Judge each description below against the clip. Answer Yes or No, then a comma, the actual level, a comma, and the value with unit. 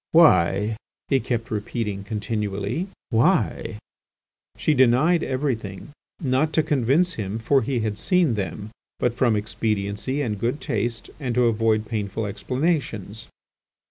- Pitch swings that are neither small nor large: Yes, average, 4.3 semitones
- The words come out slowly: Yes, slow, 125 wpm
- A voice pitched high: No, low, 115 Hz